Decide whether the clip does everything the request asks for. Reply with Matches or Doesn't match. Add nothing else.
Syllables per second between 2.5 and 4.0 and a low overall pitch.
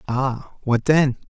Matches